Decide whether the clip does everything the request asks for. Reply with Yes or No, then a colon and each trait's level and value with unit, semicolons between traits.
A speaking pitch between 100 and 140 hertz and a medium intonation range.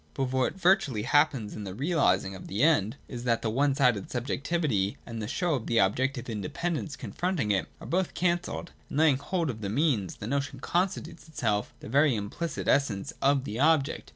No: low, 135 Hz; wide, 6.3 semitones